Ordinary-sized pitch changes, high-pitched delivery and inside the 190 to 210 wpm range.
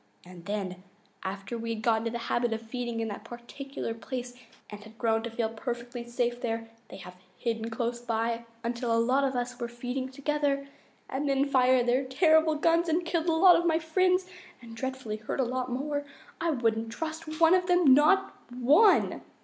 Yes: average, 4.4 semitones; high, 245 Hz; average, 195 wpm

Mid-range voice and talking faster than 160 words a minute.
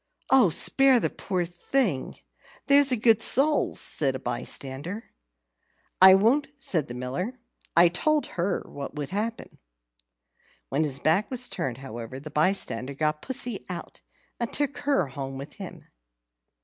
No: medium, 180 Hz; average, 145 wpm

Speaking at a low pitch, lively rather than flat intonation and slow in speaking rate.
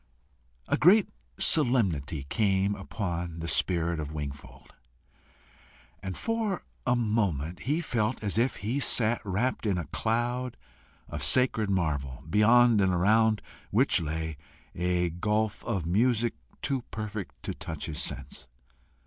Yes: low, 105 Hz; wide, 5.9 semitones; slow, 130 wpm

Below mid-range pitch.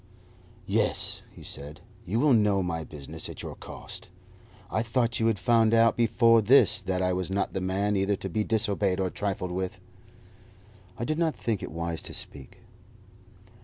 Yes: low, 100 Hz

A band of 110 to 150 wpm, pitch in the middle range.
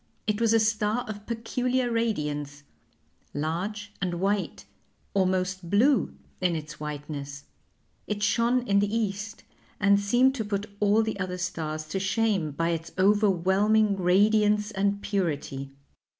No: slow, 135 wpm; high, 200 Hz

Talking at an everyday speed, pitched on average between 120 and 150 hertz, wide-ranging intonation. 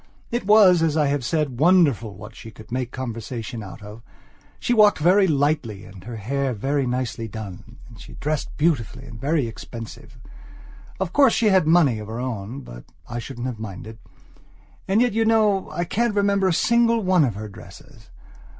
Yes: average, 185 wpm; low, 135 Hz; wide, 8.4 semitones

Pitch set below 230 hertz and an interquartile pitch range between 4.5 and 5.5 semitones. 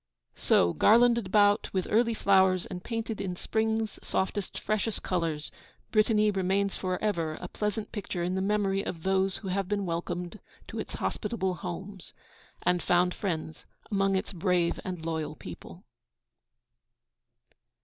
No: high, 190 Hz; average, 2.8 semitones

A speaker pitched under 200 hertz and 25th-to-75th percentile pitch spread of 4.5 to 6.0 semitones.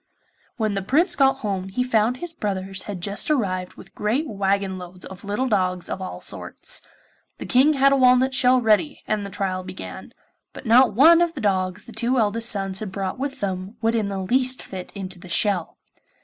No: high, 210 Hz; average, 5.0 semitones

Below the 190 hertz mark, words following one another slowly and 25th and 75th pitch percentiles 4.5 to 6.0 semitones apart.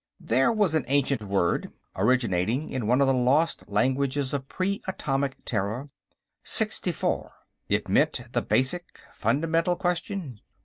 Yes: low, 135 Hz; slow, 130 wpm; average, 4.8 semitones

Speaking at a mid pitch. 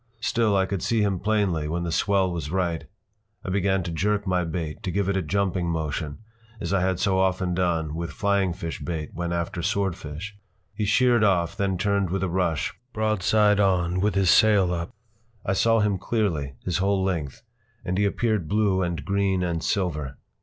No: very low, 95 Hz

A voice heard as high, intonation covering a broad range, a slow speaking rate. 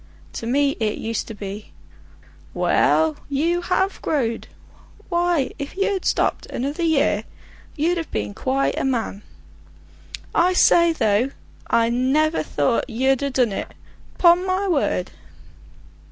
Yes: very high, 280 Hz; wide, 6.6 semitones; slow, 130 wpm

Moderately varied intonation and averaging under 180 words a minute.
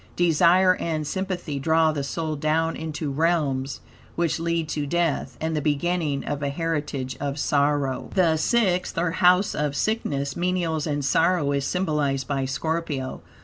Yes: average, 3.2 semitones; average, 150 wpm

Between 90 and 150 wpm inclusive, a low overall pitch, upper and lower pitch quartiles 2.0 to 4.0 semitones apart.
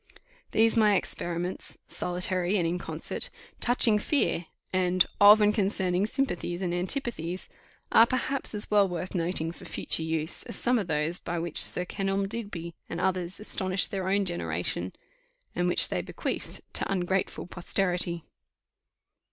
No: average, 145 wpm; medium, 185 Hz; average, 2.9 semitones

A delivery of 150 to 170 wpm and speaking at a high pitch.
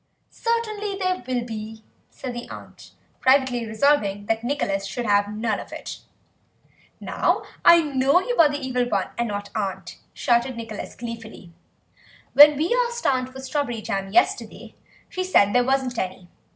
Yes: average, 160 wpm; high, 245 Hz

